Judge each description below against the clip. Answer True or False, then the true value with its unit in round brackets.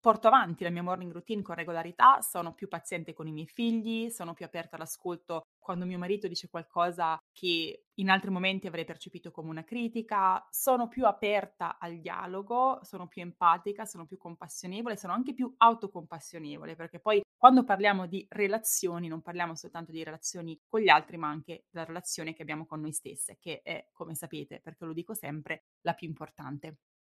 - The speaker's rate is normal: False (180 wpm)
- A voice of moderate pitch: True (175 Hz)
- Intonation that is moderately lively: True (3.6 semitones)